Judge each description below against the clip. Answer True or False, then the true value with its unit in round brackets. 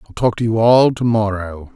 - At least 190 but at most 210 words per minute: False (240 wpm)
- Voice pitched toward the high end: False (110 Hz)